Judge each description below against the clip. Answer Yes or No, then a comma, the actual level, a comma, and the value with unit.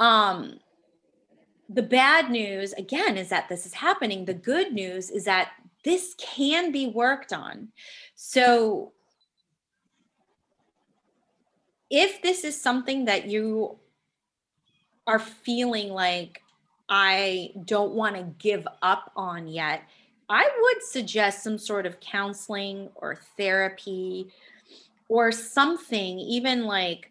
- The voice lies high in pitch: Yes, high, 215 Hz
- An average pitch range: Yes, average, 4.7 semitones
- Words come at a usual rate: No, slow, 115 wpm